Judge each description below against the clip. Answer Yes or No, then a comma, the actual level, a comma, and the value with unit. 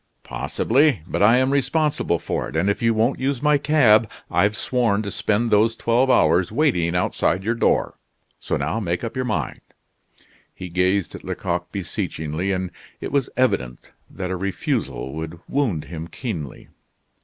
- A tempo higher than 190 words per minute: No, average, 165 wpm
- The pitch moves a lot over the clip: Yes, wide, 6.5 semitones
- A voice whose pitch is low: Yes, low, 100 Hz